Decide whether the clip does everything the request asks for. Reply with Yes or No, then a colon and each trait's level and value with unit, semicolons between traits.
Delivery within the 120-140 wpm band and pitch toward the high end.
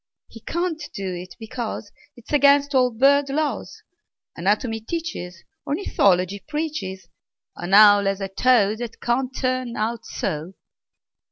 Yes: slow, 135 wpm; high, 230 Hz